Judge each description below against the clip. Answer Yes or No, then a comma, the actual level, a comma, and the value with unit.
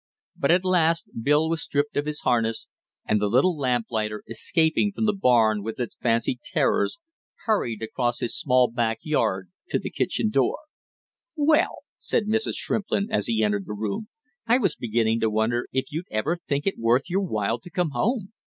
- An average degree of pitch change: No, wide, 7.8 semitones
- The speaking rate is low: No, average, 180 wpm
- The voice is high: No, low, 130 Hz